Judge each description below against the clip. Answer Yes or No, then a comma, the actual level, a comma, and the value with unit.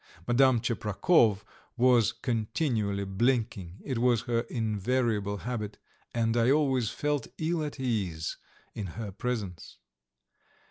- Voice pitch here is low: Yes, low, 115 Hz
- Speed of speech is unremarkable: No, slow, 110 wpm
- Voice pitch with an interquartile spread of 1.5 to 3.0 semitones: No, average, 3.6 semitones